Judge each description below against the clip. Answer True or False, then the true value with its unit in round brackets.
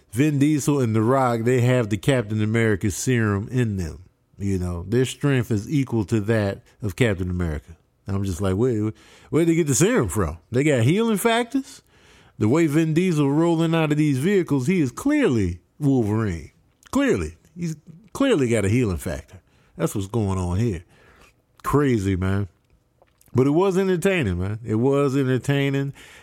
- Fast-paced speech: False (165 wpm)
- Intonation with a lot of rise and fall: True (6.6 semitones)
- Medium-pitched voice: False (125 Hz)